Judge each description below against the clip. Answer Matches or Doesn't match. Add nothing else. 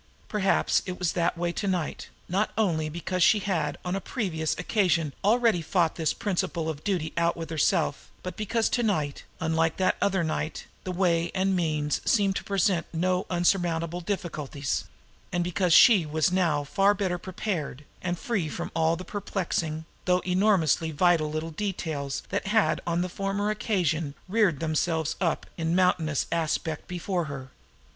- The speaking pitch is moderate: Matches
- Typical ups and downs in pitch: Matches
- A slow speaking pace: Doesn't match